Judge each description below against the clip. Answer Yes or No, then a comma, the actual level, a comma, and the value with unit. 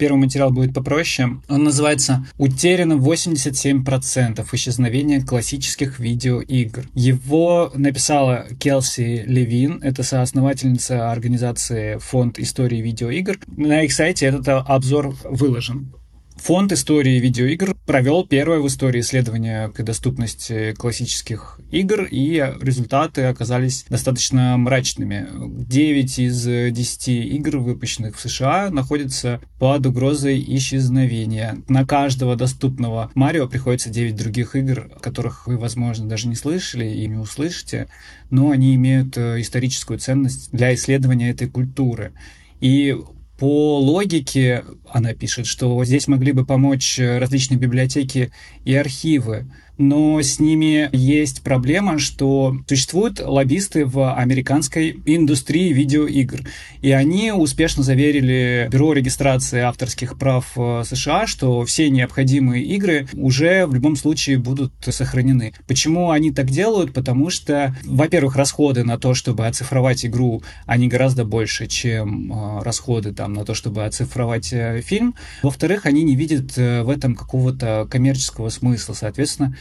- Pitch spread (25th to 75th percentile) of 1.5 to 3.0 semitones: Yes, narrow, 2.5 semitones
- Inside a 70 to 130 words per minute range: Yes, average, 120 wpm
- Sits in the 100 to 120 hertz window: No, low, 130 Hz